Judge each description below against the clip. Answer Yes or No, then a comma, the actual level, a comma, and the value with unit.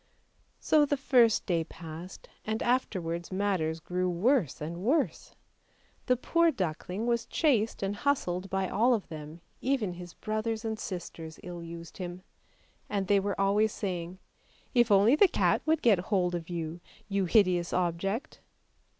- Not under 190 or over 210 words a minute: No, average, 155 wpm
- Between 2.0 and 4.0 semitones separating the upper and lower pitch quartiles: No, average, 4.6 semitones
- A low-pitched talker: No, high, 195 Hz